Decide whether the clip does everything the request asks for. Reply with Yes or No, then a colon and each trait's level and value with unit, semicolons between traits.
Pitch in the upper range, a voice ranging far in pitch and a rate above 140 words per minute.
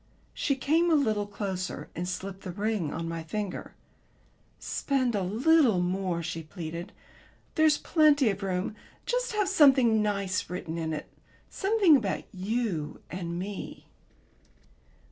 No: high, 205 Hz; wide, 7.2 semitones; slow, 135 wpm